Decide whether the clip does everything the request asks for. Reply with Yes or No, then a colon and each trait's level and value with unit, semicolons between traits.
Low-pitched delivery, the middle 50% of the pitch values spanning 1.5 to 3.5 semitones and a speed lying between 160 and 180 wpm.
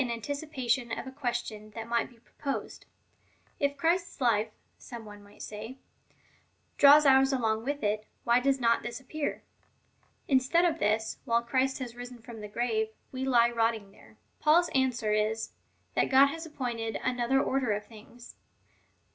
No: high, 240 Hz; average, 3.1 semitones; average, 170 wpm